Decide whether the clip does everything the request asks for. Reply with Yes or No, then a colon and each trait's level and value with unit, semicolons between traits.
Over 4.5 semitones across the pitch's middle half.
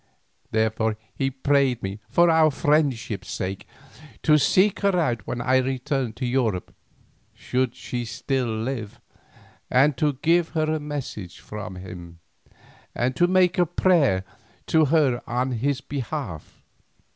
Yes: wide, 5.4 semitones